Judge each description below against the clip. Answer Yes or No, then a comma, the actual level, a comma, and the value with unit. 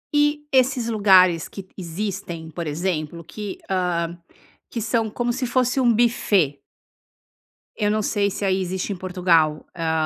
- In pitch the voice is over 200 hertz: No, high, 190 Hz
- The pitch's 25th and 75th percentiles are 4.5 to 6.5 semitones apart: Yes, average, 5.0 semitones